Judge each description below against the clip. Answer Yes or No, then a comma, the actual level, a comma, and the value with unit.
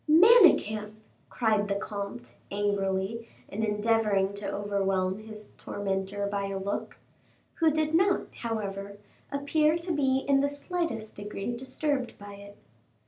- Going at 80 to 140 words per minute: Yes, slow, 135 wpm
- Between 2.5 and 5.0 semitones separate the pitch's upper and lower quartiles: No, wide, 5.4 semitones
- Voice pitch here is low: No, high, 210 Hz